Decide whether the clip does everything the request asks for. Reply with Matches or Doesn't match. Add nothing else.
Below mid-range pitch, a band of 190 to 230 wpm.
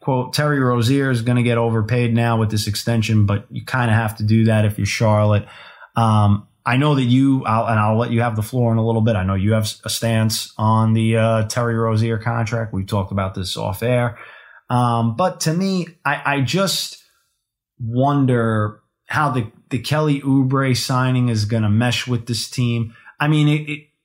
Matches